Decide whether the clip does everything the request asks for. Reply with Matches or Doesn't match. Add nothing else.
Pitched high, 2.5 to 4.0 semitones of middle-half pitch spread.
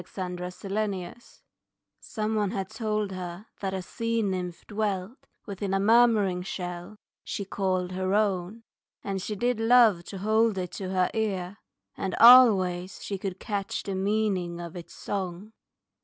Matches